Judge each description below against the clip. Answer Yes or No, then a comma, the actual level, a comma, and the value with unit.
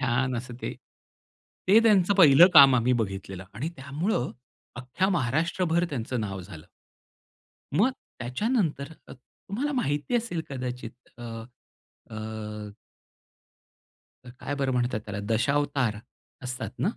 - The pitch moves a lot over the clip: Yes, wide, 5.9 semitones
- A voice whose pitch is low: Yes, low, 130 Hz